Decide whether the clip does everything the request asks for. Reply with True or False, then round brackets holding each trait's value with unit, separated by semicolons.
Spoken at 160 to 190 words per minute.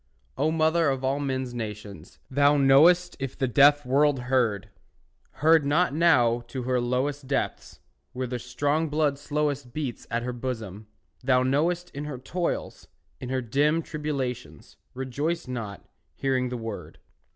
False (150 wpm)